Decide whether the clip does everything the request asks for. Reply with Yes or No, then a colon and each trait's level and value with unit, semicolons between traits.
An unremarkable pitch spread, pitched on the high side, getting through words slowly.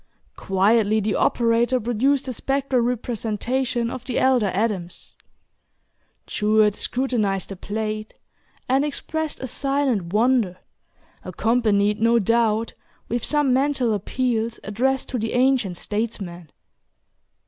Yes: average, 3.5 semitones; high, 230 Hz; slow, 110 wpm